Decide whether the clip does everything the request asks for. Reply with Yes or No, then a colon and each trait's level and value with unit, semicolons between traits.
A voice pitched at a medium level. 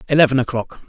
No: low, 130 Hz